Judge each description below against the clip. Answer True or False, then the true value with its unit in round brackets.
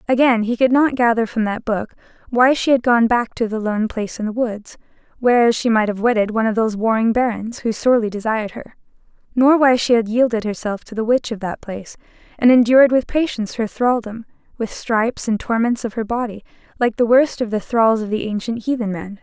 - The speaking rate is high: True (220 wpm)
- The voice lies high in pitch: True (230 Hz)